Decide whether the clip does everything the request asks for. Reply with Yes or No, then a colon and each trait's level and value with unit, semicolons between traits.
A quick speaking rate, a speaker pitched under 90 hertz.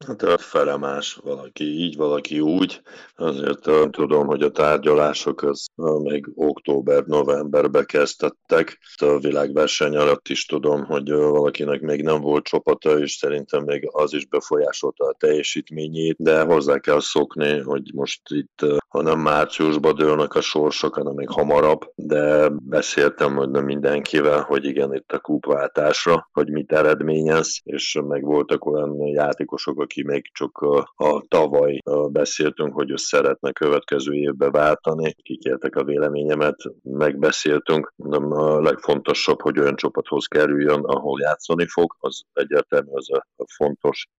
No: average, 135 wpm; very low, 75 Hz